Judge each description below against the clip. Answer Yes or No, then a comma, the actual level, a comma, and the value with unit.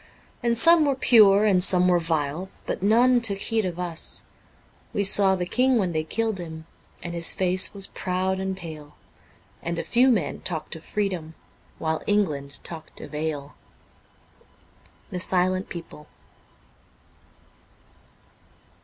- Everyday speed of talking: Yes, average, 145 wpm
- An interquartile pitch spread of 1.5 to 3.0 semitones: No, average, 4.0 semitones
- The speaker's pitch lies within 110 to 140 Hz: No, medium, 185 Hz